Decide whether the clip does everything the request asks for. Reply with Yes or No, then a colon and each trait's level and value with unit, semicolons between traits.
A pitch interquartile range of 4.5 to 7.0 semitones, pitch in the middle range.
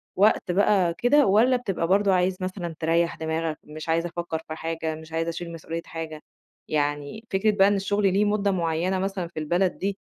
No: average, 3.3 semitones; medium, 175 Hz